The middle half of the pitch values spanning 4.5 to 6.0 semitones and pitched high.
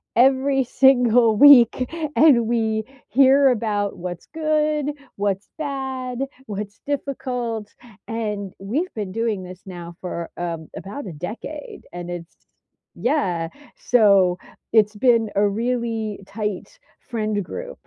Yes: average, 4.8 semitones; high, 225 Hz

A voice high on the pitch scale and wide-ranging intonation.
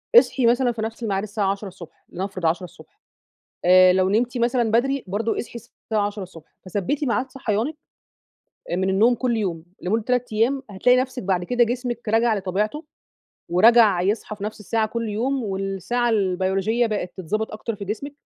No: high, 215 Hz; average, 3.9 semitones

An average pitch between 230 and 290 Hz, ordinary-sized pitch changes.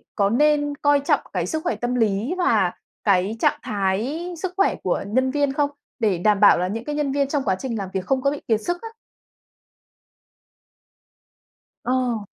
No: very high, 255 Hz; wide, 5.9 semitones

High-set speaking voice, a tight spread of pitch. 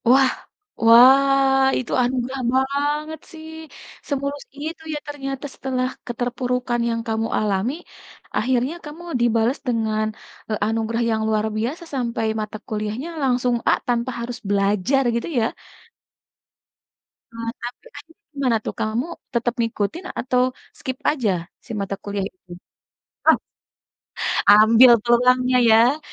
No: high, 245 Hz; average, 3.2 semitones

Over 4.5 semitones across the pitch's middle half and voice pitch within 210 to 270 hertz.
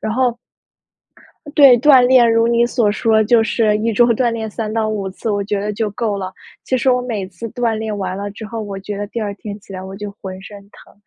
No: narrow, 2.4 semitones; high, 215 Hz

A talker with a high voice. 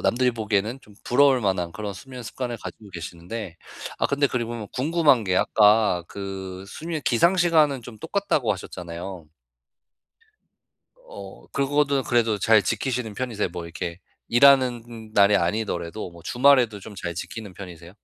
No: low, 110 Hz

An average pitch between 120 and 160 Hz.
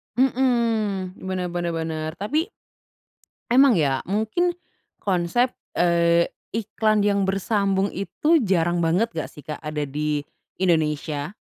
No: medium, 185 Hz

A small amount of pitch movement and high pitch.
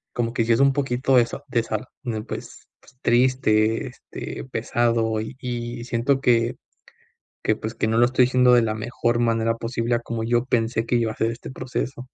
No: narrow, 1.6 semitones; low, 120 Hz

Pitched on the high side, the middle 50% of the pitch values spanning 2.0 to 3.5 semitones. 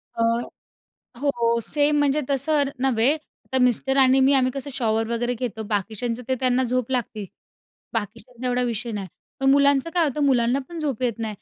Yes: very high, 250 Hz; average, 3.0 semitones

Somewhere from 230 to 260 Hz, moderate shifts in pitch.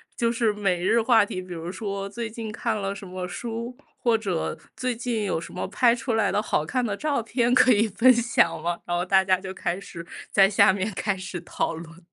No: high, 205 Hz; average, 4.1 semitones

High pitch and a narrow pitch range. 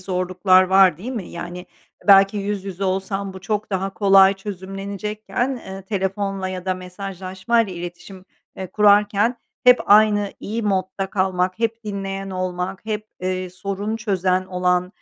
Yes: high, 195 Hz; narrow, 1.8 semitones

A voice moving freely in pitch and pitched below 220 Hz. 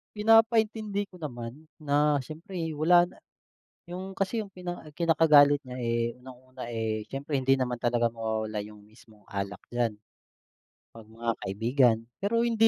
Yes: wide, 7.4 semitones; medium, 140 Hz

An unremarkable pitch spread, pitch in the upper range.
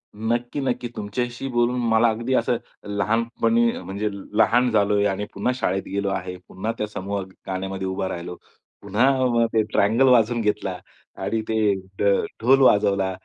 No: average, 3.4 semitones; low, 110 Hz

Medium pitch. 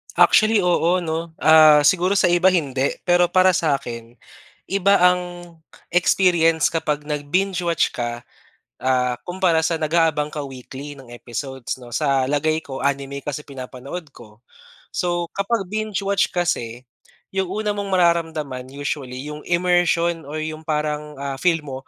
Yes: medium, 155 Hz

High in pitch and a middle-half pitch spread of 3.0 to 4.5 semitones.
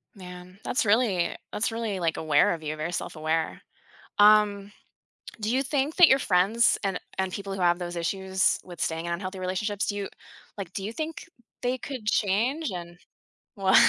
Yes: high, 195 Hz; average, 3.7 semitones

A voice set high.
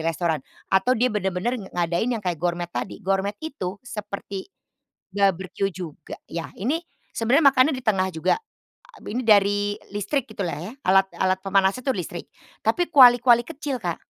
Yes: high, 200 Hz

